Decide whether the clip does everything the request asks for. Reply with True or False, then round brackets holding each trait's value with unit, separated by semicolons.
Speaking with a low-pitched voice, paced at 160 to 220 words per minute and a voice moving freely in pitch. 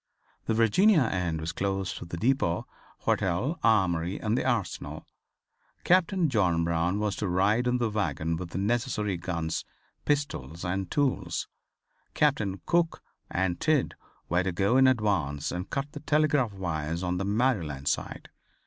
False (100 Hz; 150 wpm; 6.7 semitones)